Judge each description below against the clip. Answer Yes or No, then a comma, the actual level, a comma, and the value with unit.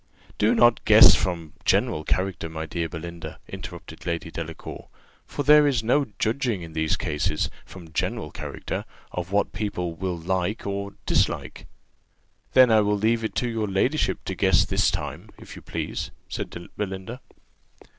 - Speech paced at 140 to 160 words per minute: Yes, average, 155 wpm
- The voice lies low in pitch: Yes, very low, 95 Hz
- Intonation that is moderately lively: Yes, average, 4.8 semitones